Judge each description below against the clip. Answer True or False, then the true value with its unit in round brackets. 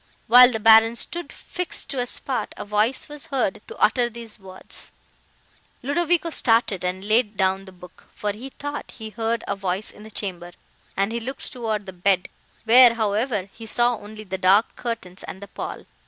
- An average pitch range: True (3.8 semitones)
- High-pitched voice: True (220 Hz)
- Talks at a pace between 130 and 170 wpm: False (185 wpm)